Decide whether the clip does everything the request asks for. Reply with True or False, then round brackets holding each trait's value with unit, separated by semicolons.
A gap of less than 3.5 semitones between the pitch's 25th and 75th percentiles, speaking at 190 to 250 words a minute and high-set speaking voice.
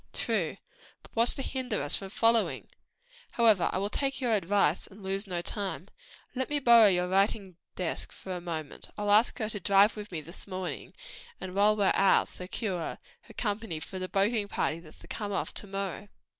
True (2.9 semitones; 195 wpm; 200 Hz)